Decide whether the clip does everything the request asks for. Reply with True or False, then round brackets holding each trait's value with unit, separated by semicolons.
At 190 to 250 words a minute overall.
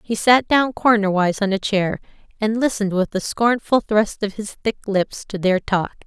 True (200 wpm)